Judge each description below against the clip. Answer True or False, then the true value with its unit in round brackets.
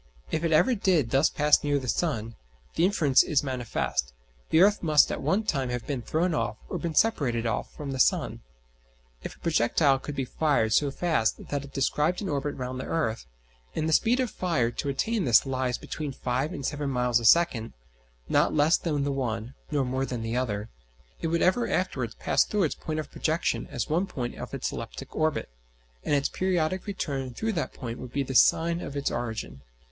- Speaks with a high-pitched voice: False (140 Hz)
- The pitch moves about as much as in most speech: True (4.7 semitones)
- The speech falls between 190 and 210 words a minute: True (205 wpm)